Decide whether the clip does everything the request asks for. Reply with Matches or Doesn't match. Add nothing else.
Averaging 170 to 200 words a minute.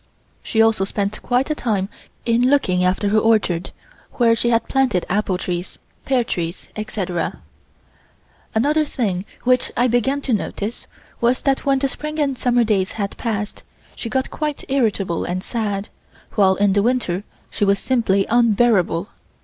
Doesn't match